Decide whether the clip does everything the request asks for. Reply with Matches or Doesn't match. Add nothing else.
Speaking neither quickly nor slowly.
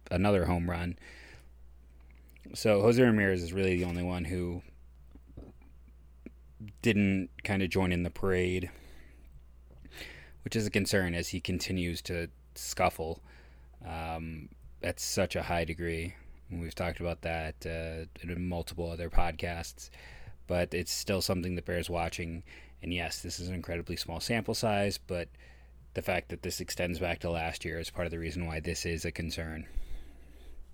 Matches